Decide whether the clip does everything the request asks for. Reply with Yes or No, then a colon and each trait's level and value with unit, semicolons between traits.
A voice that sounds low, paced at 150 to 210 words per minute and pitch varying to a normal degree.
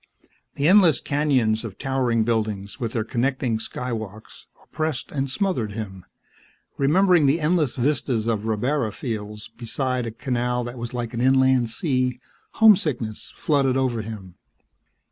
No: low, 125 Hz; slow, 135 wpm; average, 3.8 semitones